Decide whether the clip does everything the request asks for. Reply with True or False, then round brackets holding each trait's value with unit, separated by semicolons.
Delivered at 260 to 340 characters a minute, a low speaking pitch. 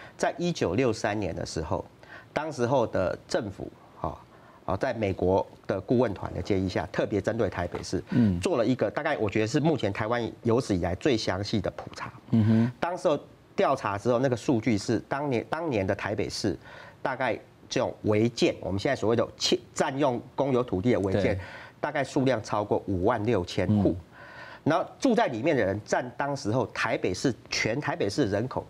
True (285 characters per minute; 115 Hz)